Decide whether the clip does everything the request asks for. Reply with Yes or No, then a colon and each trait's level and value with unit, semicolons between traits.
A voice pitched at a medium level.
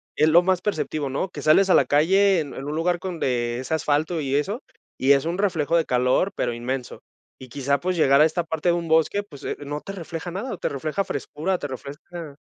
Yes: medium, 155 Hz